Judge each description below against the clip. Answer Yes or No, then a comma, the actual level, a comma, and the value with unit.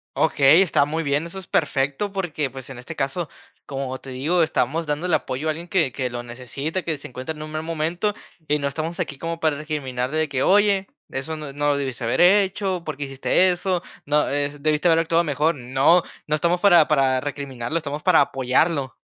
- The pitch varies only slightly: No, average, 3.6 semitones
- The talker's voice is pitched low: No, medium, 150 Hz